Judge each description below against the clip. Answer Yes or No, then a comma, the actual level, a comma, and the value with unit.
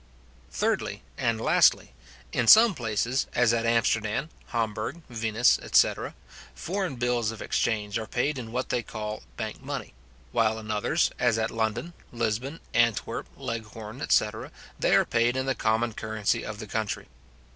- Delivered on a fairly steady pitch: Yes, narrow, 2.1 semitones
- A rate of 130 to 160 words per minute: Yes, average, 150 wpm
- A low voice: Yes, low, 115 Hz